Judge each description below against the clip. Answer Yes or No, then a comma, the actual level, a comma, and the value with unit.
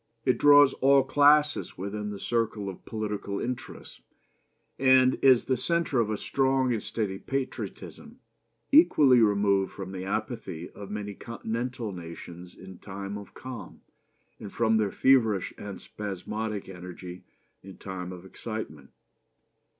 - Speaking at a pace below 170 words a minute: Yes, slow, 135 wpm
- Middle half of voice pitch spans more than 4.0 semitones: Yes, average, 4.9 semitones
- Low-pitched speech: Yes, low, 105 Hz